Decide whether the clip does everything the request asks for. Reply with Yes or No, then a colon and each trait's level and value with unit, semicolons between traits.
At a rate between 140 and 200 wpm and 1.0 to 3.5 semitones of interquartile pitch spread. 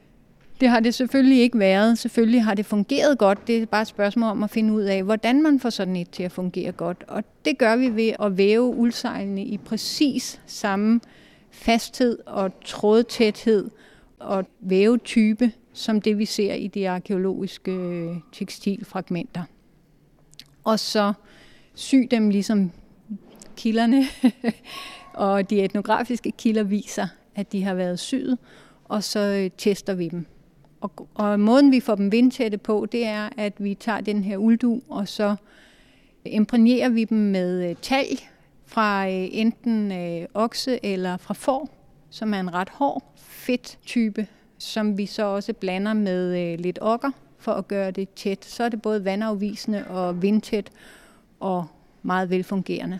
Yes: average, 150 wpm; average, 2.9 semitones